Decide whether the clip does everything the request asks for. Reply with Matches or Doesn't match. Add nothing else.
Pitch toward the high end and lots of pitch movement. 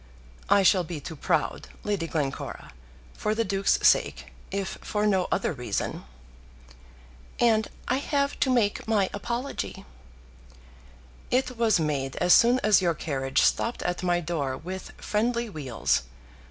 Matches